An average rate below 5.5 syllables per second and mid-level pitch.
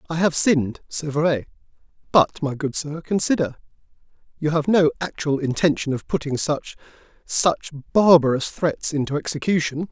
Yes: 4.9 syllables/s; medium, 155 Hz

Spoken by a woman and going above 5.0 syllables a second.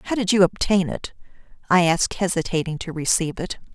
Yes: female; 5.9 syllables/s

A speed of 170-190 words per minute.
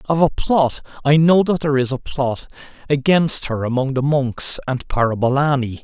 No: average, 155 wpm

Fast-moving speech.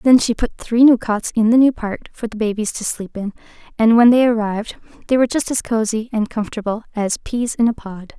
Yes: fast, 235 wpm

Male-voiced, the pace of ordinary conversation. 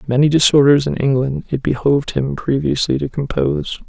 Yes: male; average, 155 wpm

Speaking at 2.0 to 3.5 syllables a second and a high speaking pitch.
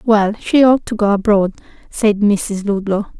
No: 4.2 syllables/s; high, 210 Hz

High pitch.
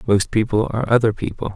No: low, 110 Hz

